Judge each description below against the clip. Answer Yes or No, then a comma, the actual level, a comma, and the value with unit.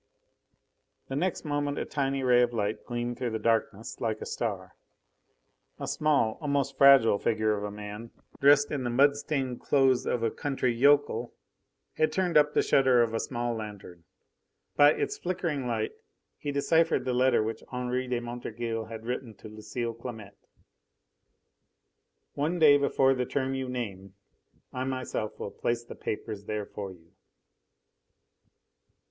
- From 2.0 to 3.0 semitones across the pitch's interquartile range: No, average, 3.8 semitones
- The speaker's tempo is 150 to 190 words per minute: Yes, average, 155 wpm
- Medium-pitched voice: No, low, 125 Hz